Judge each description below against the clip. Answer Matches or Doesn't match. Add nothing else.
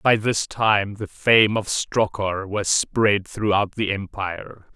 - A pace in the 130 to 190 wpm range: Matches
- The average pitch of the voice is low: Matches